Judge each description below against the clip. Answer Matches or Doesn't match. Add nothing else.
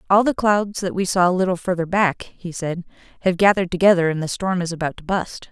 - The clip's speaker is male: Doesn't match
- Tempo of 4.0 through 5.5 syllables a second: Doesn't match